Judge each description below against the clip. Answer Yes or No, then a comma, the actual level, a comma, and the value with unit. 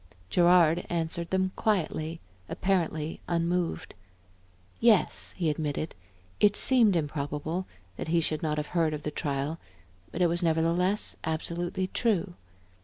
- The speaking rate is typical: No, slow, 125 wpm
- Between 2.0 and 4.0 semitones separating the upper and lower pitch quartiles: Yes, narrow, 2.6 semitones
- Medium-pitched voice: Yes, medium, 170 Hz